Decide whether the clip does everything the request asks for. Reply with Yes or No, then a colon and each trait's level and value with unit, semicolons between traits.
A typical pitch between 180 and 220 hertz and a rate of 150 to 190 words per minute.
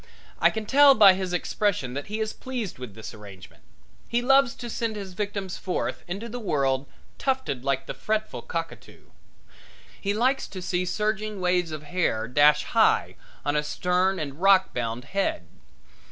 Yes: medium, 185 Hz; average, 165 wpm